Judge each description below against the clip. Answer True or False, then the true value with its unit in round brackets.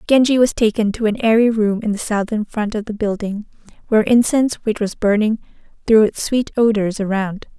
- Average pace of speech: True (190 wpm)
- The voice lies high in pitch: True (215 Hz)